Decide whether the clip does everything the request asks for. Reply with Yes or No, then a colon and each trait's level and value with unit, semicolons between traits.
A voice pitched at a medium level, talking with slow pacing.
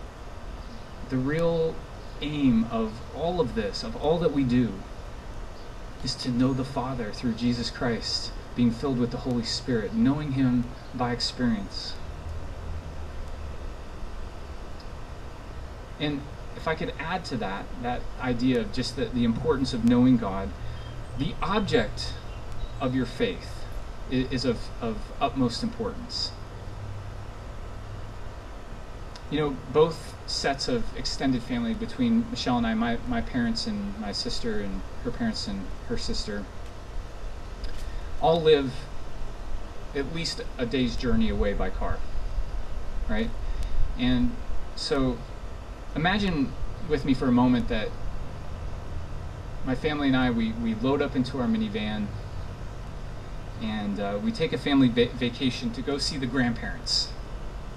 No: low, 115 Hz; slow, 130 wpm